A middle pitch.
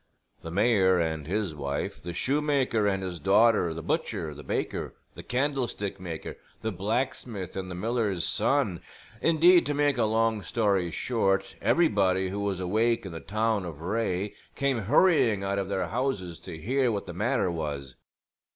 No: low, 100 Hz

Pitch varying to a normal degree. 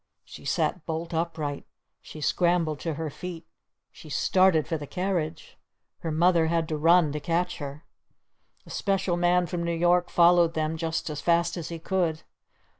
No: narrow, 1.8 semitones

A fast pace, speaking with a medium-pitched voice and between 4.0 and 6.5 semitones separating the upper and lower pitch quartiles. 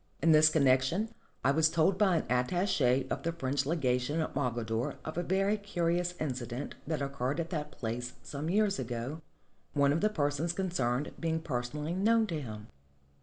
No: average, 170 wpm; medium, 150 Hz; average, 5.1 semitones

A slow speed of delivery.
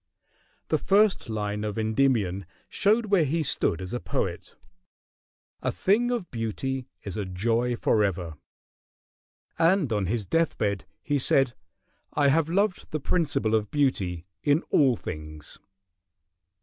Yes: slow, 130 wpm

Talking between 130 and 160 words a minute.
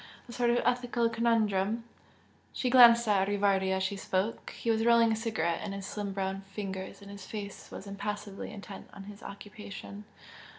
No: average, 175 wpm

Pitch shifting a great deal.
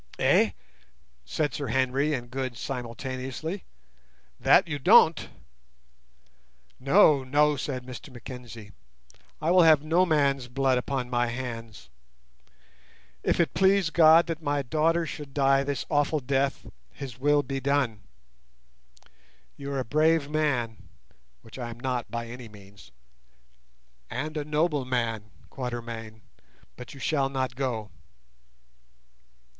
No: average, 3.5 semitones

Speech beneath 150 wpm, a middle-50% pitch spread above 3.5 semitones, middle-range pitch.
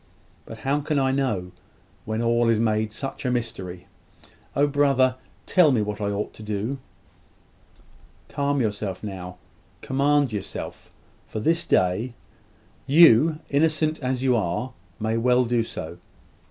No: average, 140 wpm; average, 4.7 semitones; low, 120 Hz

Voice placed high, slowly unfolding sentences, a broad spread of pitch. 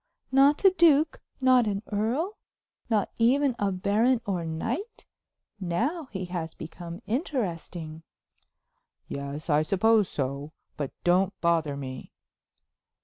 Yes: high, 200 Hz; slow, 115 wpm; wide, 7.8 semitones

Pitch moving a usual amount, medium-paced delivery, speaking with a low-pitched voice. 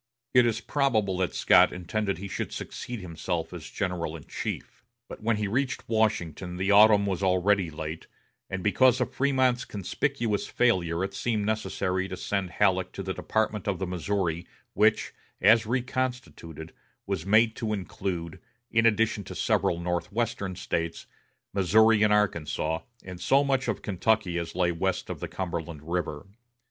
Yes: average, 4.0 semitones; average, 155 wpm; low, 100 Hz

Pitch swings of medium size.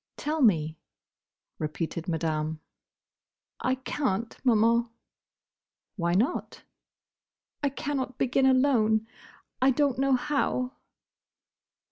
No: wide, 7.2 semitones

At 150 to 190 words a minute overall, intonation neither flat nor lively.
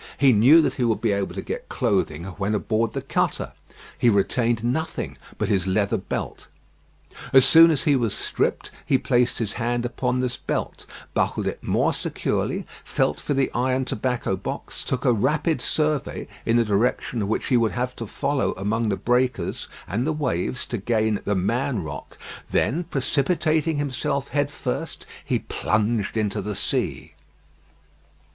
Yes: average, 165 wpm; average, 4.1 semitones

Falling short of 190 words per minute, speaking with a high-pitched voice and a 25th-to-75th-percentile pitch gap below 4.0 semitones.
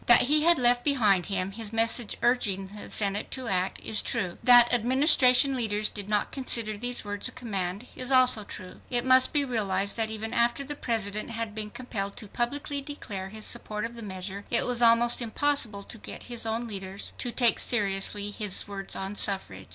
No: average, 195 wpm; high, 225 Hz; average, 3.4 semitones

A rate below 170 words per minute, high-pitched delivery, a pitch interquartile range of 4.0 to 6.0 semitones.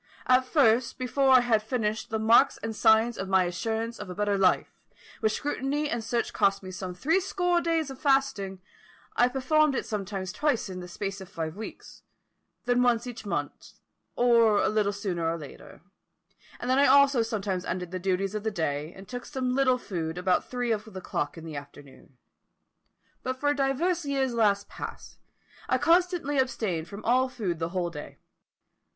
No: average, 185 wpm; high, 220 Hz; wide, 5.6 semitones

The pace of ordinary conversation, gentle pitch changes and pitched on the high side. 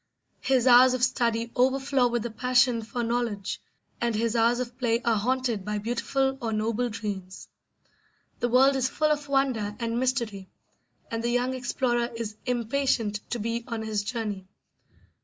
Yes: average, 160 wpm; narrow, 2.3 semitones; high, 235 Hz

